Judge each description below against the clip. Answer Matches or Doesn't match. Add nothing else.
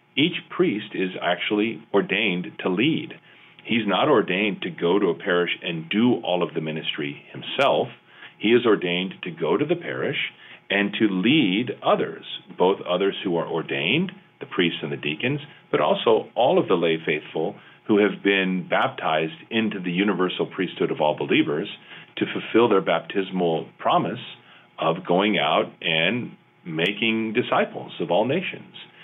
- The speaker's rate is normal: Matches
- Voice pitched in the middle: Doesn't match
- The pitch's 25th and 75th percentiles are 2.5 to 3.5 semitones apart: Doesn't match